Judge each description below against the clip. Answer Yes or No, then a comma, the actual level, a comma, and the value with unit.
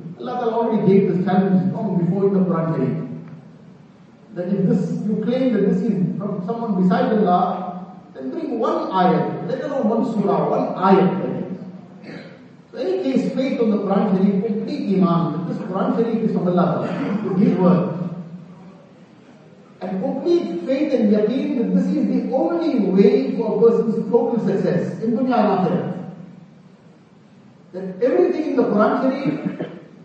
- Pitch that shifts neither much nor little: Yes, average, 3.7 semitones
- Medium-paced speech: Yes, average, 165 wpm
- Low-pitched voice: No, high, 195 Hz